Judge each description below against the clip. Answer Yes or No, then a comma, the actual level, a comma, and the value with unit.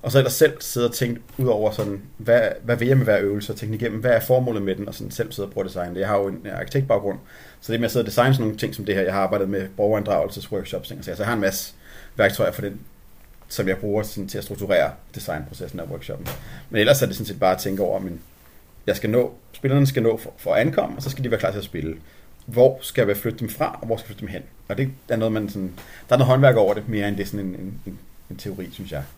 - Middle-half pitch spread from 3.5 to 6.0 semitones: Yes, average, 3.9 semitones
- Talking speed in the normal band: No, fast, 290 wpm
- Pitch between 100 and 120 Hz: Yes, low, 105 Hz